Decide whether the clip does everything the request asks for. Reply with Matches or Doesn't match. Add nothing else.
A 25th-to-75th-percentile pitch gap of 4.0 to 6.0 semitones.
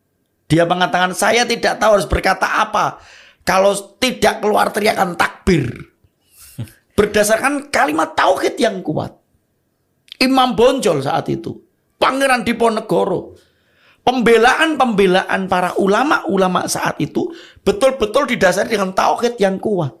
Matches